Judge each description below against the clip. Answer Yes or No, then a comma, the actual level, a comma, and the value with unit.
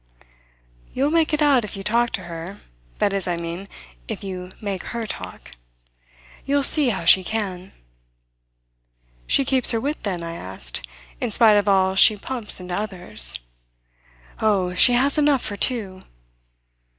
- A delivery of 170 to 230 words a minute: No, average, 155 wpm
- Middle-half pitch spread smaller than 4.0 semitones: No, average, 5.2 semitones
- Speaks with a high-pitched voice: Yes, high, 200 Hz